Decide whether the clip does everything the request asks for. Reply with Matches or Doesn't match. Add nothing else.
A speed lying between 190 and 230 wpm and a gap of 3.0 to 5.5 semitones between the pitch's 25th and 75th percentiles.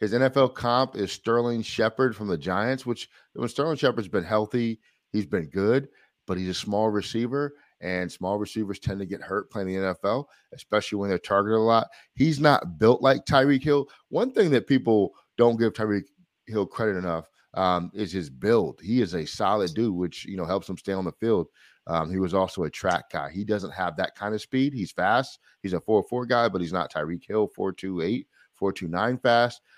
Matches